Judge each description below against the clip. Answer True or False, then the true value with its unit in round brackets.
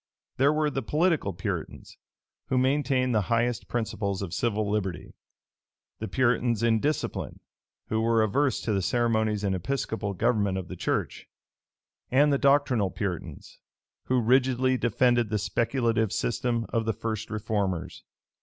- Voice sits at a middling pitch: False (115 Hz)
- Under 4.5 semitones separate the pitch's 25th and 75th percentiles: True (3.6 semitones)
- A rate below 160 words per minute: True (140 wpm)